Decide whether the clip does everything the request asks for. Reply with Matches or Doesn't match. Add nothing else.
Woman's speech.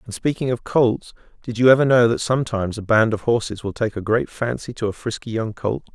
Doesn't match